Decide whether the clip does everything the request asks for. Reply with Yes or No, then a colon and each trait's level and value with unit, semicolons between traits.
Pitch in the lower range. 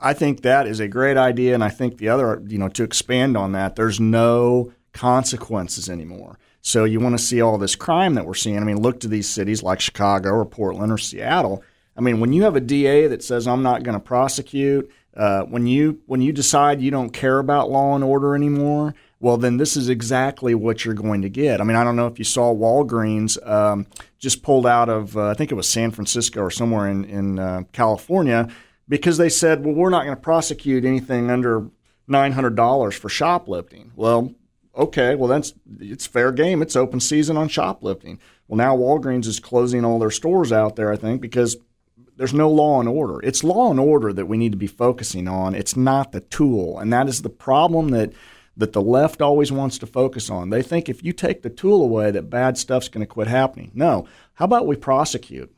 Yes: low, 120 Hz